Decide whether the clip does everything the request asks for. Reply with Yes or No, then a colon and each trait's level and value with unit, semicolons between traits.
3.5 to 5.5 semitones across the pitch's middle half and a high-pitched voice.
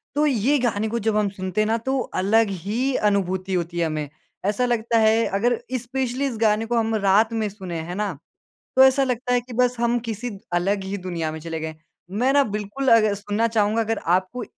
Yes: average, 3.9 semitones; high, 220 Hz